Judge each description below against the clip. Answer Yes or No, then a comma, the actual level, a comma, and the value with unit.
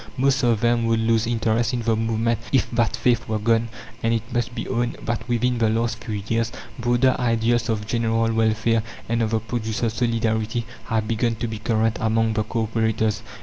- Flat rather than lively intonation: Yes, narrow, 1.0 semitones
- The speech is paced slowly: No, average, 195 wpm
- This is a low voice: Yes, low, 115 Hz